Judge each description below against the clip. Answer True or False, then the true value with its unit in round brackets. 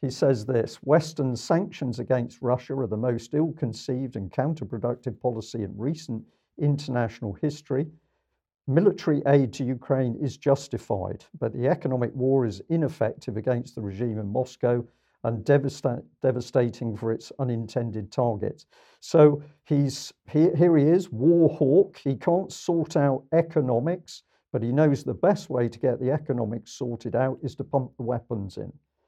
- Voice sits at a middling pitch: False (130 Hz)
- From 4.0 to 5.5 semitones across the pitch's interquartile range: False (3.6 semitones)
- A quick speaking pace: False (155 wpm)